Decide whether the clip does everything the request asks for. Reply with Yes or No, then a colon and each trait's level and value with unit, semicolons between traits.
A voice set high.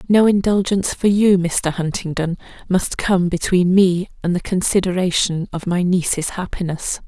No: medium, 180 Hz